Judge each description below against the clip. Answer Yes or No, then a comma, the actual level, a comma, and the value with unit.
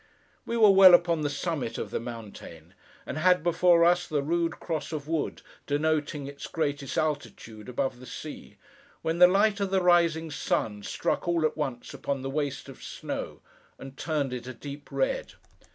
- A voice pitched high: No, medium, 155 Hz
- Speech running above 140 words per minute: Yes, average, 180 wpm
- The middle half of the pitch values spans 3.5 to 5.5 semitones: Yes, average, 4.0 semitones